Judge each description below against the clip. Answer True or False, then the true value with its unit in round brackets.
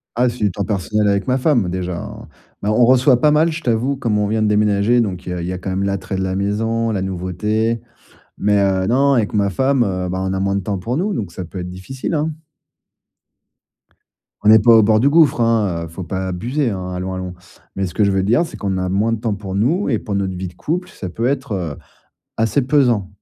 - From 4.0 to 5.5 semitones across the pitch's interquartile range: True (4.3 semitones)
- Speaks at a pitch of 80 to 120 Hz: True (105 Hz)